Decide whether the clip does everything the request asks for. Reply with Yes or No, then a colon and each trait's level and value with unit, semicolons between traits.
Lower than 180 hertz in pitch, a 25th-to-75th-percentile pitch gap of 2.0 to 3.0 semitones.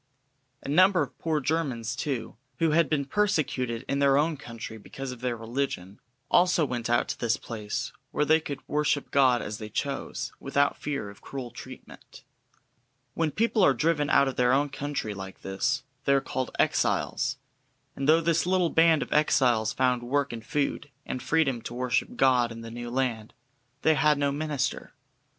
No: low, 135 Hz; average, 3.9 semitones